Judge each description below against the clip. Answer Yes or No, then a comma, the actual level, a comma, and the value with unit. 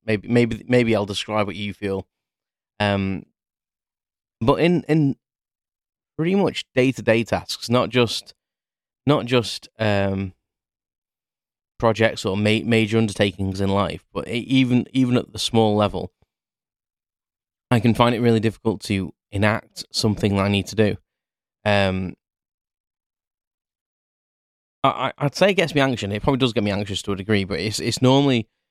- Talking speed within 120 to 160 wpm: Yes, average, 150 wpm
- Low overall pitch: Yes, low, 110 Hz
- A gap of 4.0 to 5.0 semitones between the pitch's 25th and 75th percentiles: No, average, 3.4 semitones